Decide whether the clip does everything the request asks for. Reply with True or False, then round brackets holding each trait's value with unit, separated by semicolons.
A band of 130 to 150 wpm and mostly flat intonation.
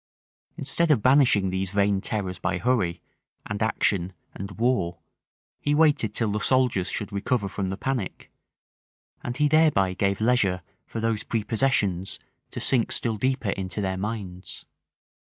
False (145 wpm; 4.6 semitones)